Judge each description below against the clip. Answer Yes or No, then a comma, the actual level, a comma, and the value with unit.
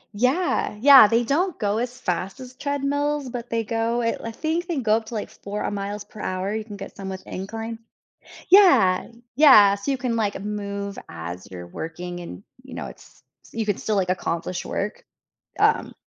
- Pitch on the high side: Yes, high, 220 Hz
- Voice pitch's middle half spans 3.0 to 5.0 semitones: Yes, average, 4.4 semitones